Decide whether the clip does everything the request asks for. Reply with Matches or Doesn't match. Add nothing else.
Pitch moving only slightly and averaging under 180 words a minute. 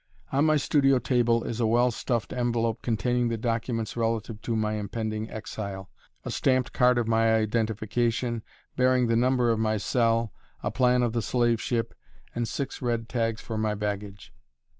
Matches